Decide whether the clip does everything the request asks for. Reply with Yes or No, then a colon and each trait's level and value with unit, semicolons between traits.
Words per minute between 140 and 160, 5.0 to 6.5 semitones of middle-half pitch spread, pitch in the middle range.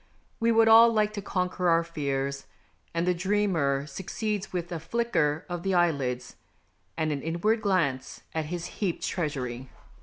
Yes: average, 155 wpm; wide, 5.4 semitones; medium, 175 Hz